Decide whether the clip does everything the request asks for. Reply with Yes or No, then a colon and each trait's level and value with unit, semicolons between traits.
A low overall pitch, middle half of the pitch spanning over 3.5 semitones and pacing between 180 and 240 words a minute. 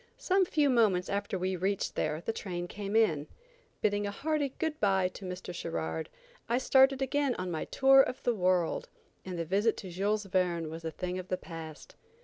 No: high, 190 Hz; average, 5.3 semitones; average, 195 wpm